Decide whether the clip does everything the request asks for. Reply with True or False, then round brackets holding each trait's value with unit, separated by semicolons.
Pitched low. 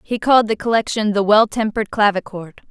False (210 Hz)